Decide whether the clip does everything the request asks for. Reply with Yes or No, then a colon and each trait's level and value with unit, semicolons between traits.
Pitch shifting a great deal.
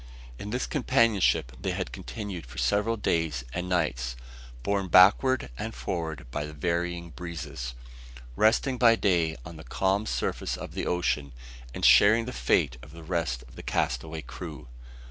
Yes: wide, 5.9 semitones